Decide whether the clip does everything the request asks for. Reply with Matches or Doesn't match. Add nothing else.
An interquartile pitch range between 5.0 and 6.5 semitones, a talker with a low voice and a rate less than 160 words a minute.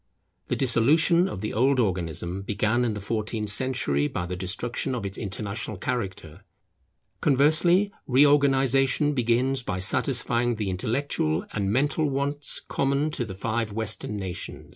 Matches